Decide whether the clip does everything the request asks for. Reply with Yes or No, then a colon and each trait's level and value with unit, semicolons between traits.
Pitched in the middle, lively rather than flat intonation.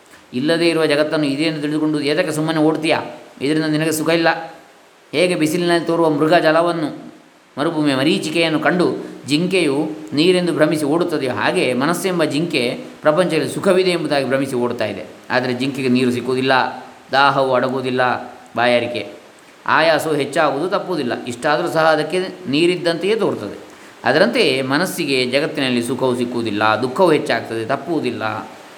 No: medium, 150 Hz; average, 4.2 semitones